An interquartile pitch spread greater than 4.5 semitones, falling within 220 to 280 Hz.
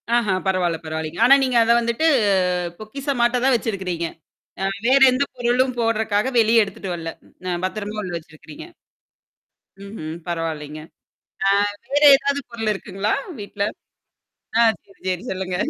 No: average, 5.0 semitones; high, 210 Hz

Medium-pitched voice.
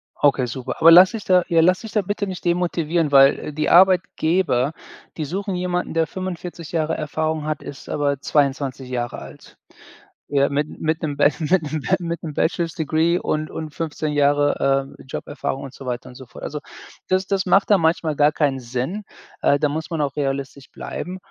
Yes: medium, 155 Hz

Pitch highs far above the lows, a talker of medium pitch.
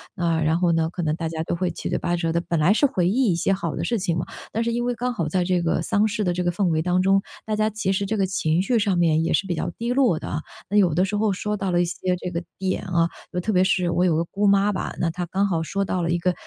No: average, 3.1 semitones; medium, 180 Hz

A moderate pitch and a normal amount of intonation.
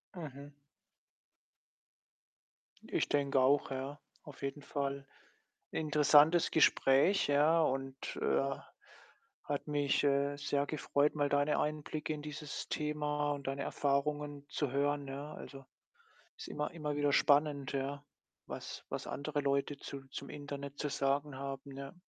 No: medium, 145 Hz; narrow, 1.2 semitones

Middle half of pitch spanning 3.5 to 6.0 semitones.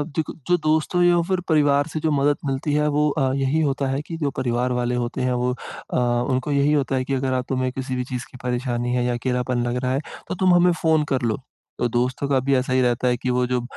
No: average, 3.0 semitones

